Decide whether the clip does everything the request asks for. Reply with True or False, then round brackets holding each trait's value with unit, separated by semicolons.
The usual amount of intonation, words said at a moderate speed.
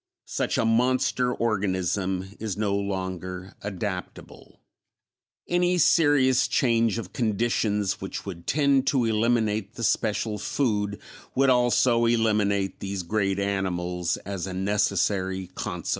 False (3.6 semitones; 115 wpm)